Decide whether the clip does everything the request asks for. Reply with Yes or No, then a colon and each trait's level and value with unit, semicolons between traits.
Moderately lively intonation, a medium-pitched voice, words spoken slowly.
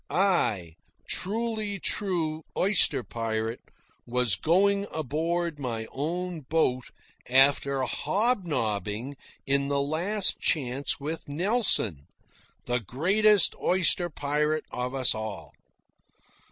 No: wide, 6.5 semitones; medium, 150 Hz; slow, 100 wpm